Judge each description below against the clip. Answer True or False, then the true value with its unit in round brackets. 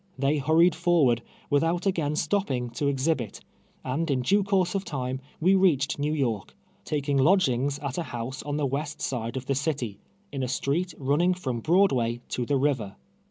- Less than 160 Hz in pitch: True (140 Hz)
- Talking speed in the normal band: True (180 wpm)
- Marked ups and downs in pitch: False (4.3 semitones)